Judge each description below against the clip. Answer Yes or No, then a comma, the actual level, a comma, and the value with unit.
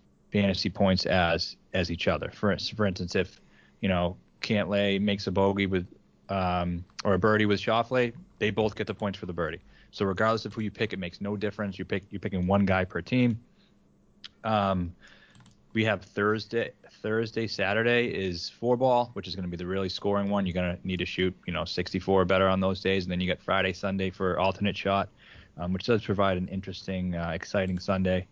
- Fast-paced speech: Yes, fast, 210 wpm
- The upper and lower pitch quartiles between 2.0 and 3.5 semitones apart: Yes, narrow, 2.4 semitones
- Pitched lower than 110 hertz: Yes, very low, 95 Hz